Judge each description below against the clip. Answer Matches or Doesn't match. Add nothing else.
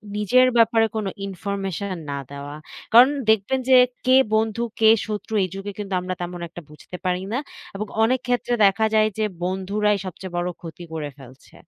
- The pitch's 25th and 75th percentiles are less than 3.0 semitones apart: Doesn't match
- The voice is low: Doesn't match